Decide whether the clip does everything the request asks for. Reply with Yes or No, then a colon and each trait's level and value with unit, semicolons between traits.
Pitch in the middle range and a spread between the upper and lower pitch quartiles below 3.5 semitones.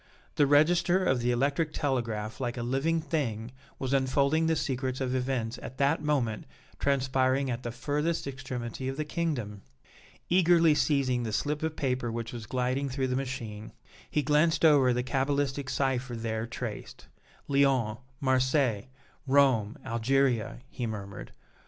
No: low, 130 Hz; average, 3.0 semitones